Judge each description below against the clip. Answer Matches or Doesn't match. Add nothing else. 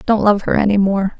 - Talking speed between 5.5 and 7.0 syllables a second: Matches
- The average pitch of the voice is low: Doesn't match